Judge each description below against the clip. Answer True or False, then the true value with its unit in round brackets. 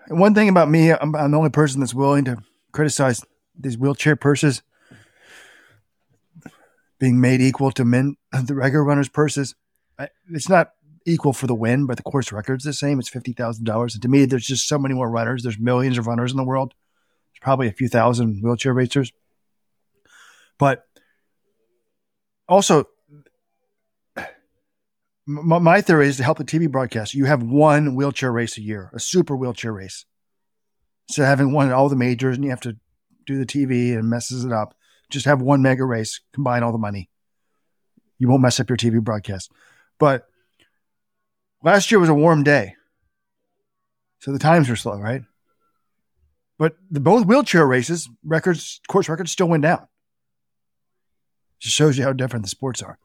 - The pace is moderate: True (170 wpm)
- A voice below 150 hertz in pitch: True (135 Hz)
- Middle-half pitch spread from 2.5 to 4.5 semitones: True (4.0 semitones)